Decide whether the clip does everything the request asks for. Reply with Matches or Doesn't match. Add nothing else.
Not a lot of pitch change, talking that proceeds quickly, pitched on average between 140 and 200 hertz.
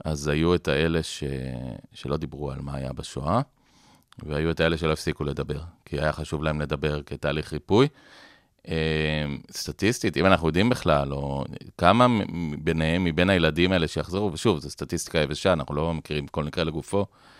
Doesn't match